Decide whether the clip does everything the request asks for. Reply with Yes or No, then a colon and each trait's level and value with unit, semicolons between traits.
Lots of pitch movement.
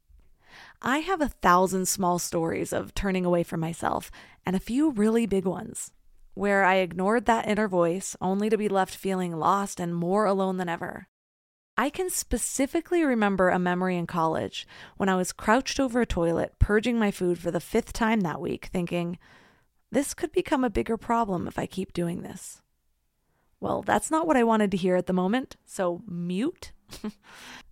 No: average, 4.5 semitones